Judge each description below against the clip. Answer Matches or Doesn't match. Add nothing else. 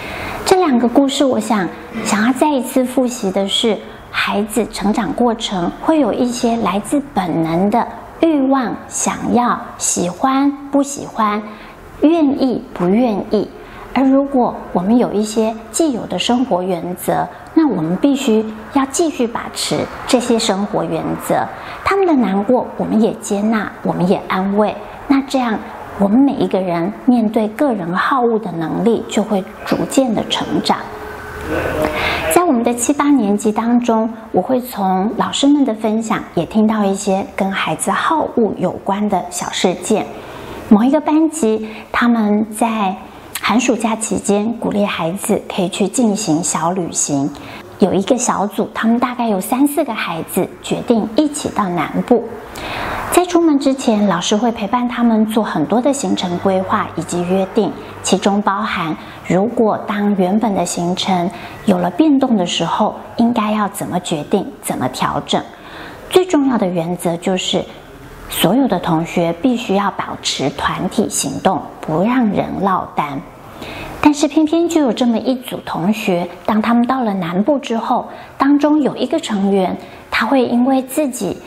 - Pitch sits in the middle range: Doesn't match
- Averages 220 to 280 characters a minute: Matches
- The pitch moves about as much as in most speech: Matches